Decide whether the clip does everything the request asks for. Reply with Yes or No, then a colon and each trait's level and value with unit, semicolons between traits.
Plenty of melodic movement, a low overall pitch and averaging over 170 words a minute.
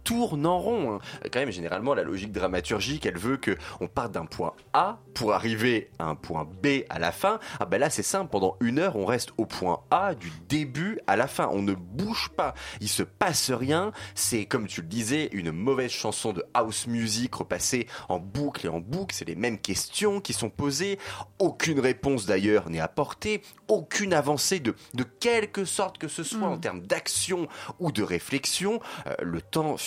Yes: wide, 7.8 semitones; low, 125 Hz; average, 200 wpm